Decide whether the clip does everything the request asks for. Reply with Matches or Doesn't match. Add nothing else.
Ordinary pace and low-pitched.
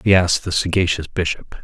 Matches